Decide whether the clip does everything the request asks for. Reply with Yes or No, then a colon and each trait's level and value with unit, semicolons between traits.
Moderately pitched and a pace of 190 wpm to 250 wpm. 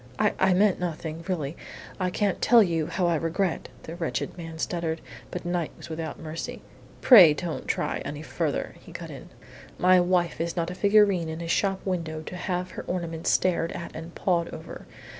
Yes: medium, 170 Hz; average, 195 wpm